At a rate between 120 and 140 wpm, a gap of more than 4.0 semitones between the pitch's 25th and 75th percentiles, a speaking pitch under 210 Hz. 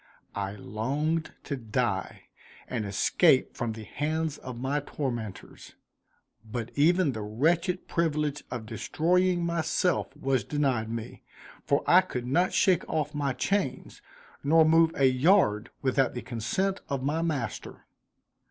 Yes: slow, 135 wpm; wide, 5.5 semitones; medium, 140 Hz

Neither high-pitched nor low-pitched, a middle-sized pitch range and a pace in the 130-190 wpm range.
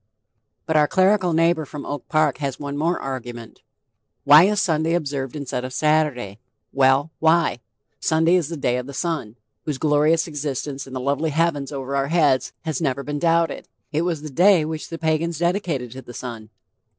Yes: medium, 150 Hz; average, 3.4 semitones; average, 185 wpm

